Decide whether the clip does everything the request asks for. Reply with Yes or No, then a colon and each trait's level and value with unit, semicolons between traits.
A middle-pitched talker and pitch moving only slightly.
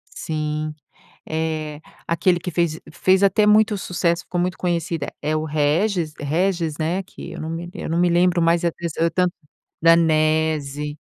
Yes: medium, 165 Hz; narrow, 2.3 semitones